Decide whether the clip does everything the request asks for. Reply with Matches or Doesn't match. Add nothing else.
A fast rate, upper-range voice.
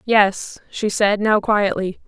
Doesn't match